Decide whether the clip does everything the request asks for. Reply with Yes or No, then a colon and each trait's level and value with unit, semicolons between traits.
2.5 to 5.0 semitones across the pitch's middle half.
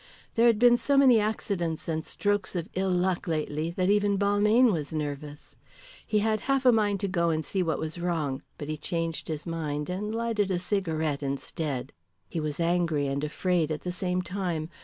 Yes: average, 4.6 semitones